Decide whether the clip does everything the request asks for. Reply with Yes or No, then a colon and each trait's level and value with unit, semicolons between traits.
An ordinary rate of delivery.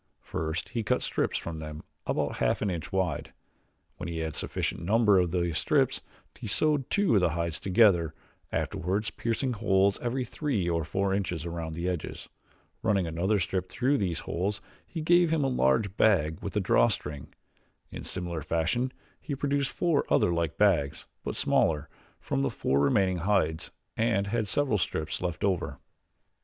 Yes: average, 165 wpm